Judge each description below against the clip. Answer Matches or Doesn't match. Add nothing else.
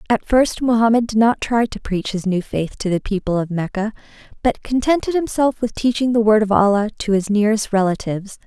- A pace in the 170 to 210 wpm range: Matches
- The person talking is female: Matches